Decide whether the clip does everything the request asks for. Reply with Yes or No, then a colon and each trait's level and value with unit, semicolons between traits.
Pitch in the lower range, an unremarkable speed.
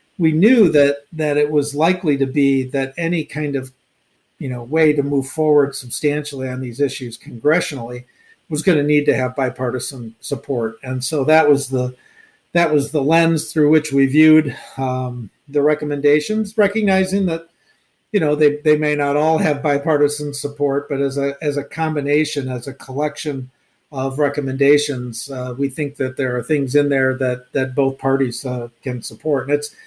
No: medium, 145 Hz; average, 180 wpm